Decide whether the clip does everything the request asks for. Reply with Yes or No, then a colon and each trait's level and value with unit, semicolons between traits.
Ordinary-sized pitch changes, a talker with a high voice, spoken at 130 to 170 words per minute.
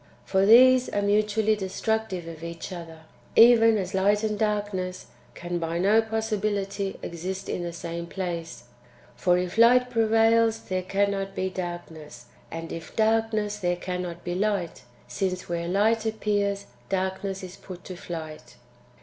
Yes: average, 3.5 semitones; high, 195 Hz; average, 145 wpm